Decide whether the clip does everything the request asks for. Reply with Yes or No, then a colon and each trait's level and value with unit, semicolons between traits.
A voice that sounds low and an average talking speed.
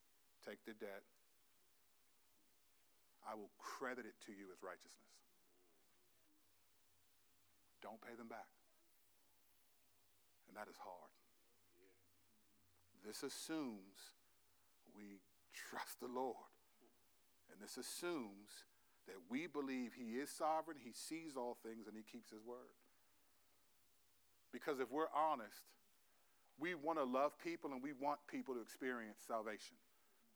No: low, 110 Hz; slow, 115 wpm